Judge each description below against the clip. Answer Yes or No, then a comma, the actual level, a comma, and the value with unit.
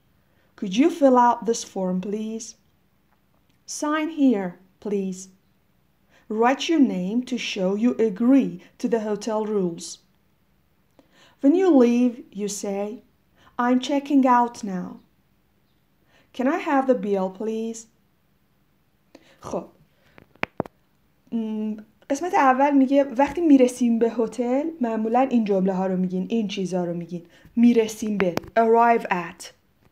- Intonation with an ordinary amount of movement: Yes, average, 4.2 semitones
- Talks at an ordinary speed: Yes, average, 115 wpm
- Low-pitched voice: No, high, 230 Hz